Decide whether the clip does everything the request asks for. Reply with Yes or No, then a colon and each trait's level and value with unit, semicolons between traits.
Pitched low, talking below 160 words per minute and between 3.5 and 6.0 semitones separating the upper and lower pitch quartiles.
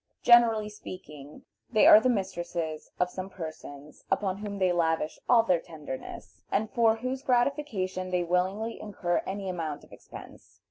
No: medium, 185 Hz; average, 150 wpm; average, 4.4 semitones